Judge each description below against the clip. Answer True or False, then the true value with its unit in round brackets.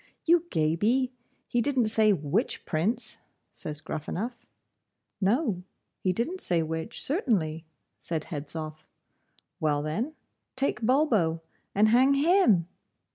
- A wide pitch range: True (8.0 semitones)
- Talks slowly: True (110 wpm)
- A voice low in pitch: False (210 Hz)